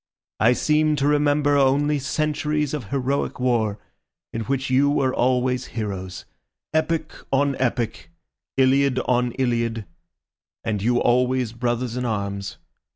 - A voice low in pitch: Yes, low, 130 Hz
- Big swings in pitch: No, average, 3.3 semitones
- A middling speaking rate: No, slow, 120 wpm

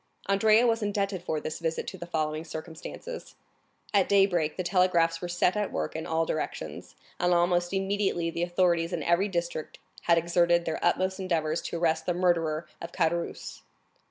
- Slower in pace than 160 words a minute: No, average, 170 wpm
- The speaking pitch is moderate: Yes, medium, 175 Hz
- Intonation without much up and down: Yes, narrow, 2.3 semitones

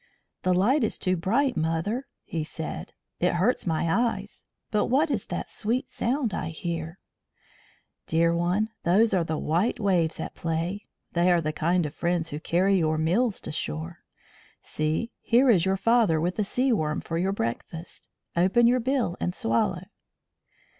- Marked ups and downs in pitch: Yes, wide, 5.7 semitones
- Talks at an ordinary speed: Yes, average, 165 wpm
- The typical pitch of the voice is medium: Yes, medium, 180 Hz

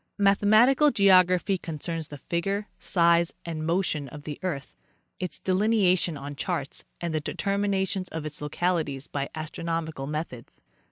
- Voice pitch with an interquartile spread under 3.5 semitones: No, average, 4.0 semitones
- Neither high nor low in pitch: Yes, medium, 170 Hz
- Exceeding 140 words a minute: No, slow, 135 wpm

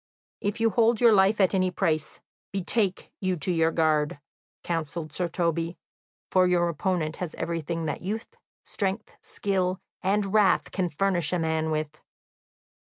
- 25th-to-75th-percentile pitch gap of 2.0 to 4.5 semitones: Yes, average, 3.2 semitones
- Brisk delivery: No, average, 150 wpm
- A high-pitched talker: No, medium, 180 Hz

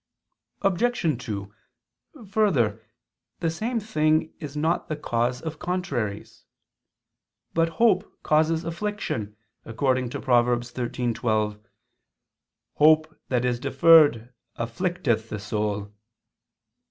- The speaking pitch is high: No, low, 135 Hz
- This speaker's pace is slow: Yes, slow, 95 wpm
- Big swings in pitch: Yes, wide, 6.2 semitones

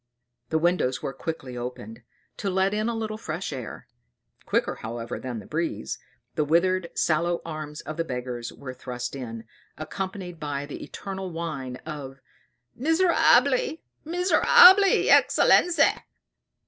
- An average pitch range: No, wide, 6.9 semitones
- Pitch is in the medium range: Yes, medium, 160 Hz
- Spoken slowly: Yes, slow, 130 wpm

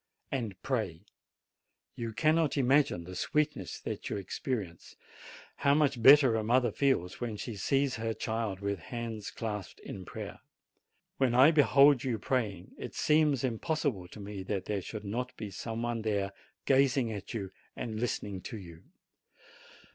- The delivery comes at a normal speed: Yes, average, 155 wpm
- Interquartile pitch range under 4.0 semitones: No, average, 4.9 semitones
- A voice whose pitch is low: Yes, low, 115 Hz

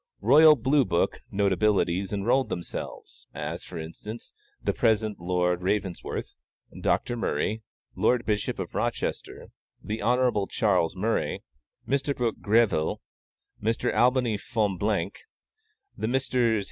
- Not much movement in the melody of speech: No, average, 4.4 semitones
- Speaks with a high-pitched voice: No, low, 110 Hz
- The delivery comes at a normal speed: No, slow, 110 wpm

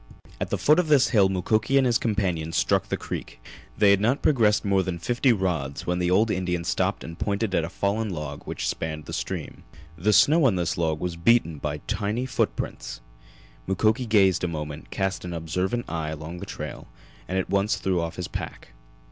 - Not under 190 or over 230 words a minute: Yes, average, 200 wpm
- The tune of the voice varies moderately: Yes, average, 4.5 semitones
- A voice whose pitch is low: Yes, very low, 95 Hz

